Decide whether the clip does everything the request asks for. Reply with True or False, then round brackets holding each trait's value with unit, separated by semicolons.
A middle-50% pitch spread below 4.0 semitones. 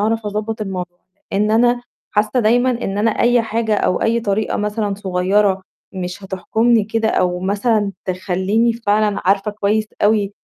True (2.4 semitones)